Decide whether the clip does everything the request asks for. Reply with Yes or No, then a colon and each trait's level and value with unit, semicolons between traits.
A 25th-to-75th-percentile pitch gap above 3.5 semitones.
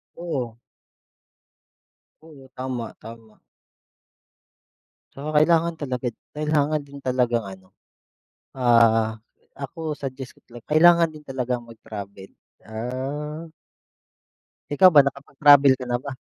Yes: average, 4.0 semitones